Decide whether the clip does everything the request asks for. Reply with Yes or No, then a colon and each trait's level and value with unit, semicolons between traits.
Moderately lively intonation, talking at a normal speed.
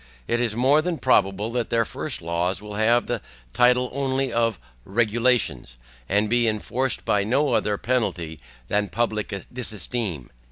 Yes: average, 3.3 semitones; average, 150 wpm